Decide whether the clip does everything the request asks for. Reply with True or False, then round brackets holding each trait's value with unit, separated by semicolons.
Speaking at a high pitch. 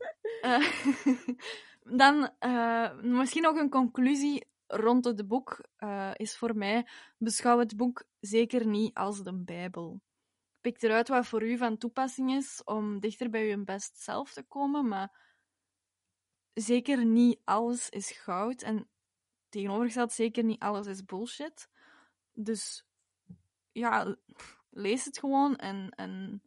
True (230 Hz)